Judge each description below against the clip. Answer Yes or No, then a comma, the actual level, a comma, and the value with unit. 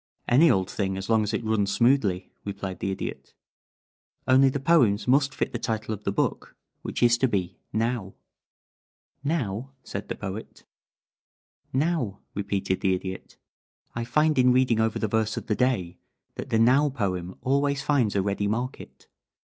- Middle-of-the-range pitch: No, low, 110 Hz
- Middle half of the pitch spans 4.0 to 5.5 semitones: Yes, average, 4.8 semitones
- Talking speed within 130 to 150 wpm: No, average, 165 wpm